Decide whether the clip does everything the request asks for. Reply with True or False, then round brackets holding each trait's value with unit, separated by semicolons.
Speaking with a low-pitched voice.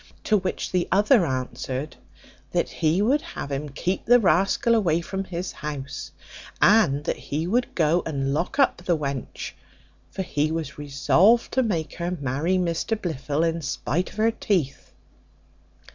False (170 Hz)